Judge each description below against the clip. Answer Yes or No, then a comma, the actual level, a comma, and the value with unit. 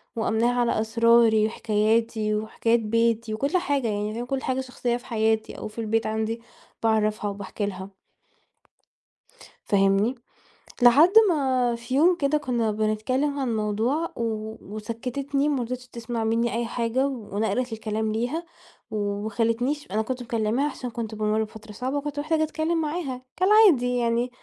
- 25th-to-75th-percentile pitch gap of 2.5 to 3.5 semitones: Yes, average, 3.2 semitones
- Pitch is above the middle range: Yes, high, 235 Hz